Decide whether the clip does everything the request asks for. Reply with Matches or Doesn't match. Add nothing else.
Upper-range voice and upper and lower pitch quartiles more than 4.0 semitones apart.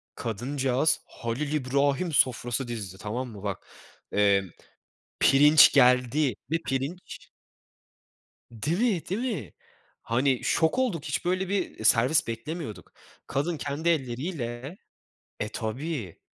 Doesn't match